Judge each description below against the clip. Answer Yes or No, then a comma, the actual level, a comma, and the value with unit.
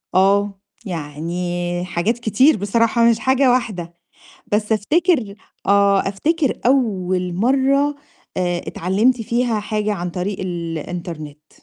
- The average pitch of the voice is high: Yes, high, 205 Hz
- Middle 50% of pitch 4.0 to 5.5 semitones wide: Yes, average, 5.1 semitones